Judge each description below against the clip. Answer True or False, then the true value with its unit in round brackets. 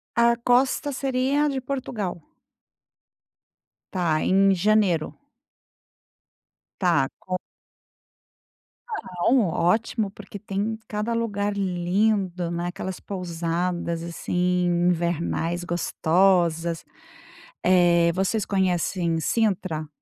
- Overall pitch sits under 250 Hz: True (185 Hz)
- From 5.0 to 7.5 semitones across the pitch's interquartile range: False (3.6 semitones)